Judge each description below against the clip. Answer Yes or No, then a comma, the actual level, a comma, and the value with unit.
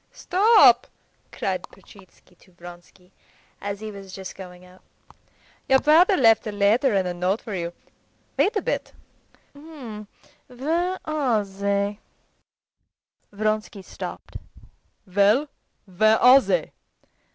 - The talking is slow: Yes, slow, 115 wpm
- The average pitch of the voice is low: No, high, 215 Hz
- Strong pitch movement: Yes, wide, 5.7 semitones